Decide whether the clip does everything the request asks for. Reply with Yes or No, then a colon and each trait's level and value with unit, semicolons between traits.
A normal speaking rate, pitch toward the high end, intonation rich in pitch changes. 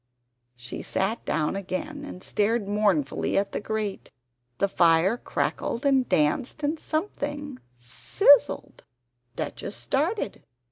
No: slow, 125 wpm; high, 215 Hz; wide, 7.6 semitones